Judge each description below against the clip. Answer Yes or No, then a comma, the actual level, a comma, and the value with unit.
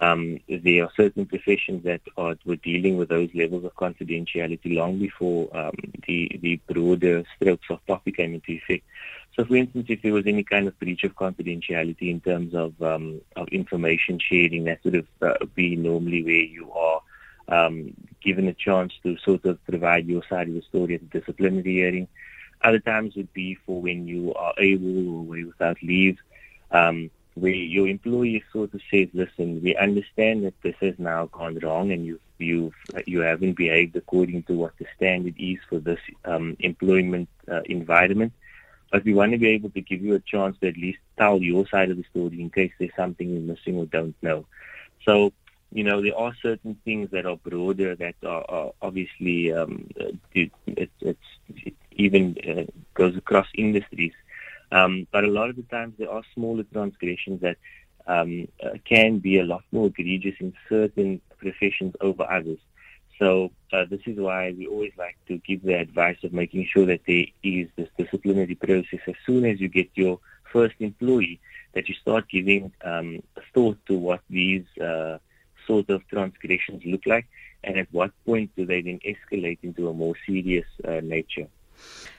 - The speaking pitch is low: Yes, very low, 90 Hz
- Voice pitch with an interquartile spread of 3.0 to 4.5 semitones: No, narrow, 2.4 semitones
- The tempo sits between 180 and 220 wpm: Yes, average, 185 wpm